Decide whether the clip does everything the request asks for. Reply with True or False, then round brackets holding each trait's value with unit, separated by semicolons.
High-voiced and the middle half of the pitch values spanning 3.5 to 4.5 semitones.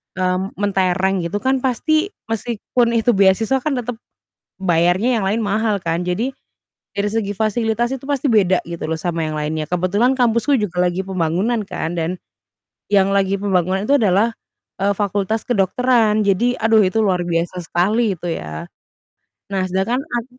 True (200 Hz; 4.2 semitones)